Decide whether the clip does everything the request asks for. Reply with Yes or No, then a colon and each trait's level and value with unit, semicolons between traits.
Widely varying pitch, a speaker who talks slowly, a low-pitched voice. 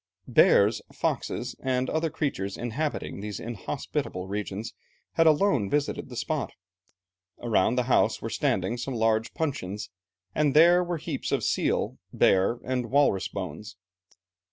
Yes: wide, 6.0 semitones; slow, 130 wpm; low, 125 Hz